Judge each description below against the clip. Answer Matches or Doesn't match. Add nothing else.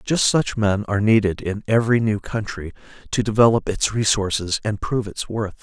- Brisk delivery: Doesn't match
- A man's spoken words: Matches